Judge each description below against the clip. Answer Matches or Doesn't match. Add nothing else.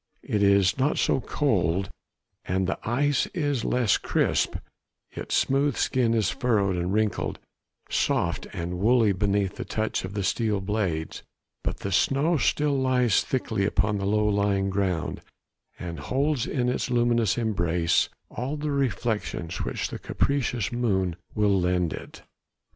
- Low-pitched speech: Matches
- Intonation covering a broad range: Doesn't match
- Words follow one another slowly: Doesn't match